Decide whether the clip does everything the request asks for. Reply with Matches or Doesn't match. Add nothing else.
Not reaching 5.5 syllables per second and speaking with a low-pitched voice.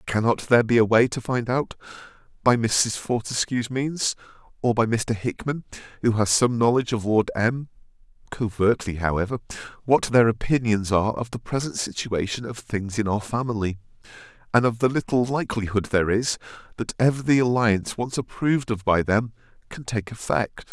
Matches